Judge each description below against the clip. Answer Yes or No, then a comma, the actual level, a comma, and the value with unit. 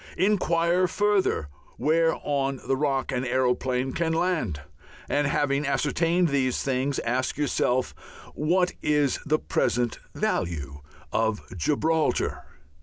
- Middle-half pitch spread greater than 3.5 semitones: Yes, average, 4.3 semitones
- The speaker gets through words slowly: Yes, slow, 110 wpm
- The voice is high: No, medium, 140 Hz